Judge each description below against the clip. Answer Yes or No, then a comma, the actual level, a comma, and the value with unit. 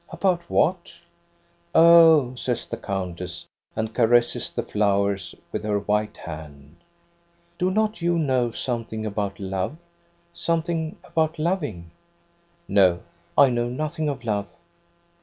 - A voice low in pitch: Yes, low, 125 Hz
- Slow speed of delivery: Yes, slow, 130 wpm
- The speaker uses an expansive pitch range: Yes, wide, 8.9 semitones